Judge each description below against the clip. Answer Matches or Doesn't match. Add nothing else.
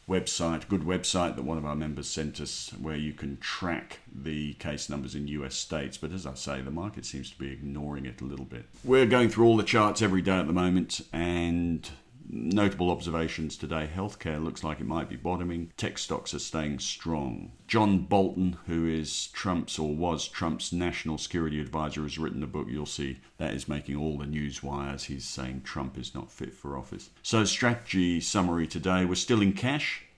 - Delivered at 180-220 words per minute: Matches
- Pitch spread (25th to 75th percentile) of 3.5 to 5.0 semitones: Matches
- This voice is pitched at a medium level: Doesn't match